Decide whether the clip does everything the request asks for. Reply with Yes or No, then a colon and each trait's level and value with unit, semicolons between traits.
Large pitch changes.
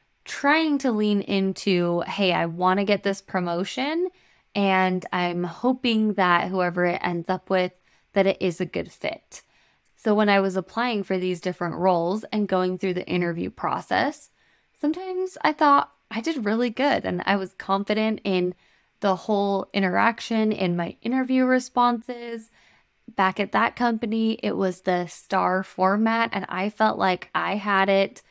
No: average, 3.7 semitones